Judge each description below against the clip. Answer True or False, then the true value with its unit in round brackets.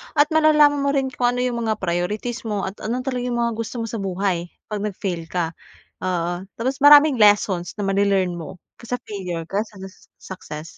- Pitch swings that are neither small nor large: True (5.0 semitones)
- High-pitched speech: True (210 Hz)